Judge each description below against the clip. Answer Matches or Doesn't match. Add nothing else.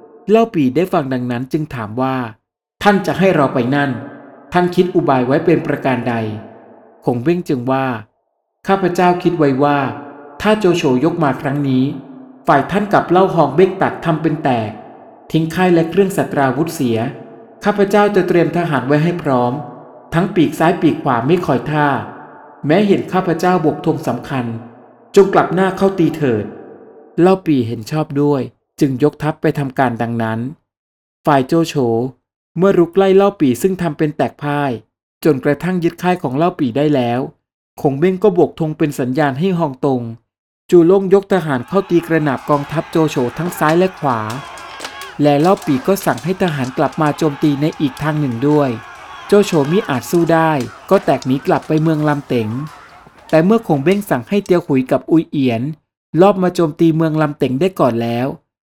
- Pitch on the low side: Doesn't match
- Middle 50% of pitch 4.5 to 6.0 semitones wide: Matches